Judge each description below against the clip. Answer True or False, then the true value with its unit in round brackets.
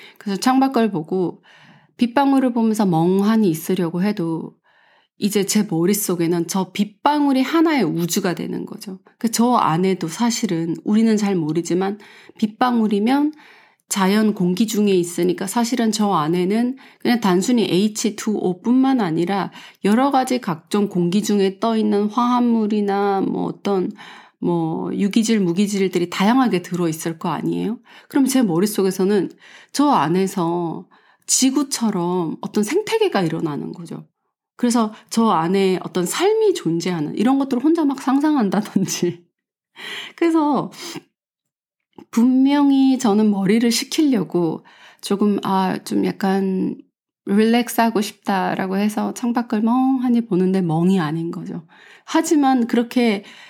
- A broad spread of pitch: False (4.9 semitones)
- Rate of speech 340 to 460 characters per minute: False (280 characters per minute)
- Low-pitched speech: False (210 Hz)